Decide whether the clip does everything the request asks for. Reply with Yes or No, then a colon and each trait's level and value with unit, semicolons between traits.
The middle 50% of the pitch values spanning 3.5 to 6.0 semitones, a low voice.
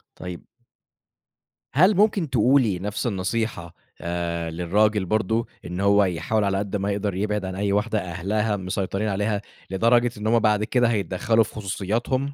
No: average, 3.0 semitones; low, 105 Hz